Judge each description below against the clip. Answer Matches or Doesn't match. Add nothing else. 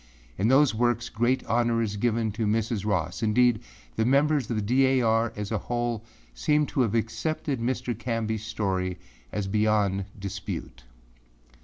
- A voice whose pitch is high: Doesn't match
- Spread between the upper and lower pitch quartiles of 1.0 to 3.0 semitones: Matches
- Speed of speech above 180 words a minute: Doesn't match